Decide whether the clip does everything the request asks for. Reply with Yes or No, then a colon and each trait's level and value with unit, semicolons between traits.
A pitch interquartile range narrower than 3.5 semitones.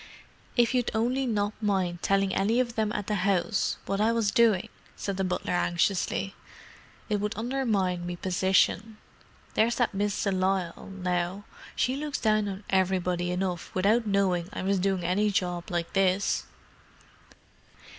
Yes: average, 2.8 semitones